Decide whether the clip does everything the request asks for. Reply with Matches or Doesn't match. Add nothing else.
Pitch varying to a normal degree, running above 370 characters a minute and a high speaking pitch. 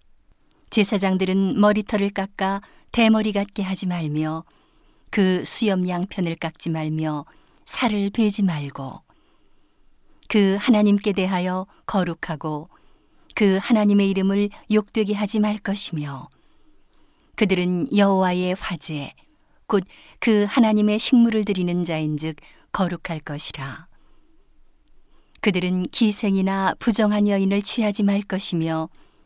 Doesn't match